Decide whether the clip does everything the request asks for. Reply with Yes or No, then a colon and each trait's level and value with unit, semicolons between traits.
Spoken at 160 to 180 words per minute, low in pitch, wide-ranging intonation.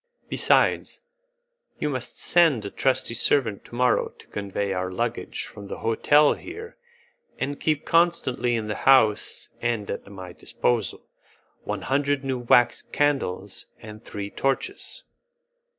No: slow, 135 wpm; low, 120 Hz; wide, 5.7 semitones